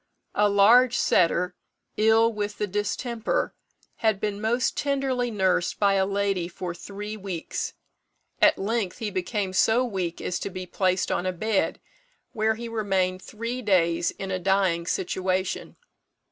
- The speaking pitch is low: No, high, 200 Hz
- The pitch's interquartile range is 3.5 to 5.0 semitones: No, average, 3.1 semitones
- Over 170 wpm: No, average, 145 wpm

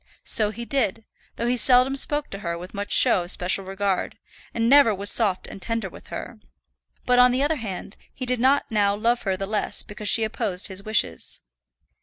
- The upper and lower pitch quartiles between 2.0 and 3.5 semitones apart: No, average, 4.0 semitones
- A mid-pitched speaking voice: No, high, 215 Hz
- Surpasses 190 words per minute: Yes, fast, 205 wpm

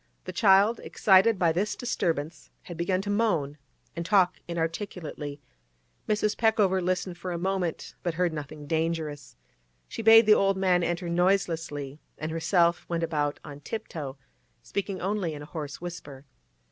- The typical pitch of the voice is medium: Yes, medium, 175 Hz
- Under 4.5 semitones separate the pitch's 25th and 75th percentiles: Yes, average, 3.6 semitones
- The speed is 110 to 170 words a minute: Yes, average, 155 wpm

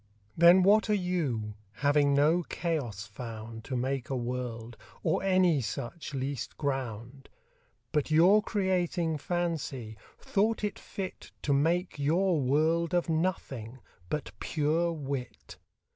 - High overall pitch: No, medium, 150 Hz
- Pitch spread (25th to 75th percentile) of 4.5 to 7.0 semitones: Yes, wide, 5.5 semitones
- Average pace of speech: No, slow, 125 wpm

